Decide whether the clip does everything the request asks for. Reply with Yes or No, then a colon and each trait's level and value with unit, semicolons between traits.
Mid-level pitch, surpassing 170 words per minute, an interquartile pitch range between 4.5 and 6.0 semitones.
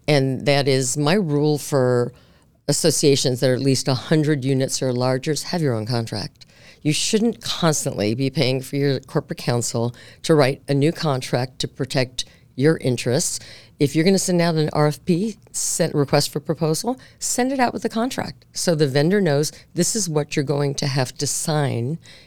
No: medium, 145 Hz; average, 185 wpm; average, 3.4 semitones